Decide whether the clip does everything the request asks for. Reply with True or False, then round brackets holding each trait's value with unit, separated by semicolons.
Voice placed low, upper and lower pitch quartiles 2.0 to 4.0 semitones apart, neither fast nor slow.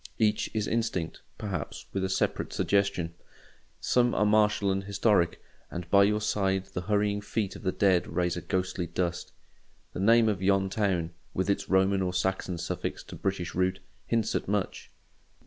True (95 Hz; 2.4 semitones; 165 wpm)